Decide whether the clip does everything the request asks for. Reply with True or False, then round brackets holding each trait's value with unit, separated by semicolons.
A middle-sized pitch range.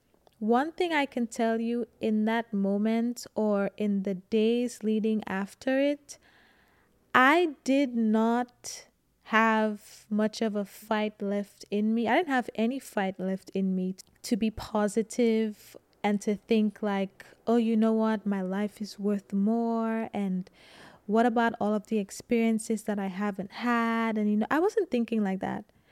False (2.2 semitones)